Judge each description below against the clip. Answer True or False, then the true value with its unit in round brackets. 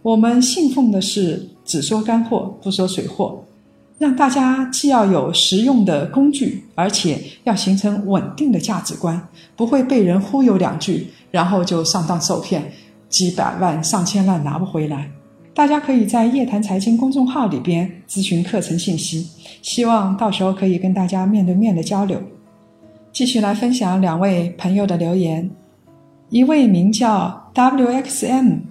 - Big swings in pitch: False (4.9 semitones)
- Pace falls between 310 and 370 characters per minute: False (245 characters per minute)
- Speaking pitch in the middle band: False (195 Hz)